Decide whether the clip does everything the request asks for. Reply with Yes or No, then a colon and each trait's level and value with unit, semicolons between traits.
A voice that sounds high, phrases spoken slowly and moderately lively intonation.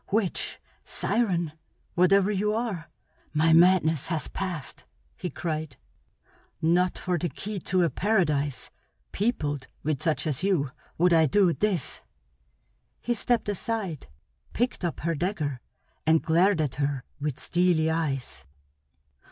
No: medium, 170 Hz; slow, 125 wpm; average, 4.0 semitones